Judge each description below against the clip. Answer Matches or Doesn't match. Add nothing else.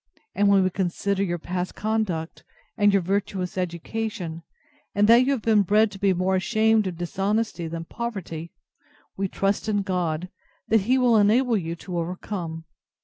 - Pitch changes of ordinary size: Matches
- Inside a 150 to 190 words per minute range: Matches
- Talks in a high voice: Matches